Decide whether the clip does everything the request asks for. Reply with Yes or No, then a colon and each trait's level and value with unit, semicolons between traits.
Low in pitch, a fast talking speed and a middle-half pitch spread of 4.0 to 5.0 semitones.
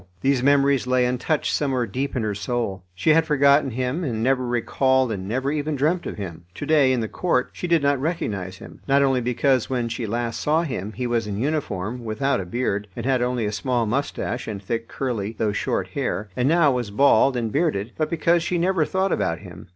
Yes: low, 125 Hz; fast, 220 wpm; average, 4.3 semitones